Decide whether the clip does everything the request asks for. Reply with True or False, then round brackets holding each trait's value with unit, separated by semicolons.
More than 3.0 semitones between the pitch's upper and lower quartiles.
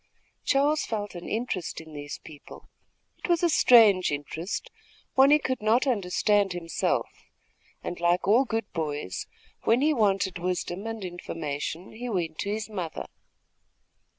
True (5.1 semitones)